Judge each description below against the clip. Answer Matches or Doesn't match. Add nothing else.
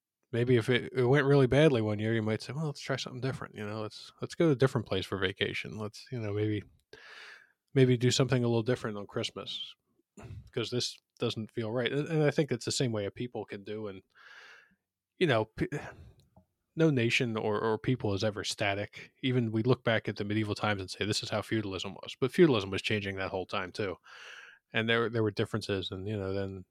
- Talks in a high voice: Doesn't match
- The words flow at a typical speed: Doesn't match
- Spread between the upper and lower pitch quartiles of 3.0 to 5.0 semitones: Matches